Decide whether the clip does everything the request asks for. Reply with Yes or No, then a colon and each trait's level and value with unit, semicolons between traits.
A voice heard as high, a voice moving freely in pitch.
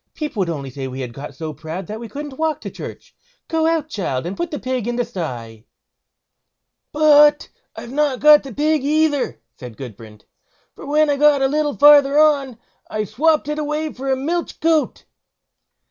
Yes: very high, 275 Hz; wide, 9.0 semitones